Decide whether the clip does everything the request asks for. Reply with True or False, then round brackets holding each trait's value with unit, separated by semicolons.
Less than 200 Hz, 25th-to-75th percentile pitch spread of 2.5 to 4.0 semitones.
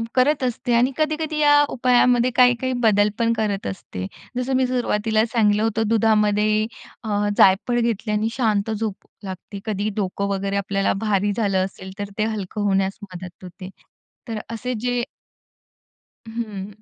False (215 Hz; 3.2 semitones)